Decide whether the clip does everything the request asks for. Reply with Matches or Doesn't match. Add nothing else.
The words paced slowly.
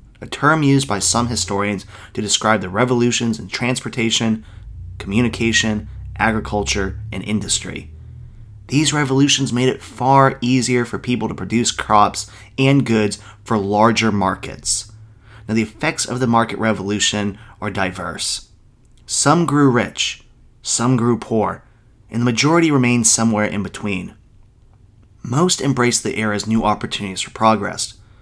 Matches